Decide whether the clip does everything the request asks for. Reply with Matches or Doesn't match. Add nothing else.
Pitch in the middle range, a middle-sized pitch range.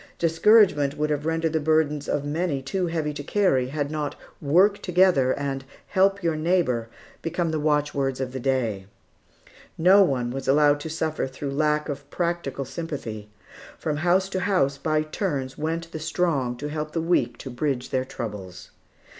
Matches